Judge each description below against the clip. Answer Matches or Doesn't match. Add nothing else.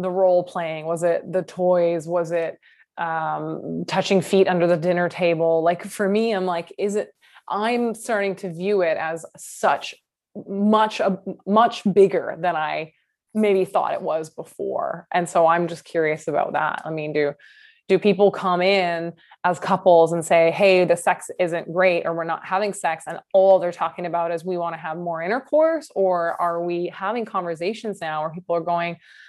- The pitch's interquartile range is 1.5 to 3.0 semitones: Matches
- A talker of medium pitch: Matches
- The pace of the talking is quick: Doesn't match